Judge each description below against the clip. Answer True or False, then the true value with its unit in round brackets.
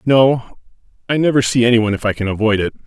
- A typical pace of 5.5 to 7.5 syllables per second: True (6.5 syllables/s)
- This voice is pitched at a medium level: False (115 Hz)